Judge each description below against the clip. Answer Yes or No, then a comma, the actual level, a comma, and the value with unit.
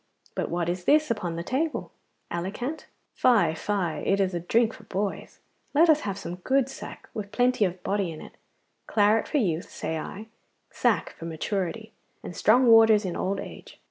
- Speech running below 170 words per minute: No, average, 180 wpm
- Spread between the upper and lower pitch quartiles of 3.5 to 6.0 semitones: Yes, average, 4.7 semitones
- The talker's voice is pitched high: Yes, high, 200 Hz